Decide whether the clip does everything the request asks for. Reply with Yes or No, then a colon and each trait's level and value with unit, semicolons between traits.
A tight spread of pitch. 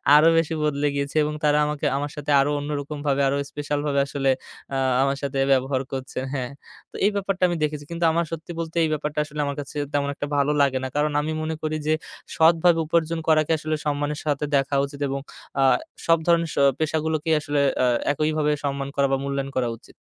Yes: narrow, 2.0 semitones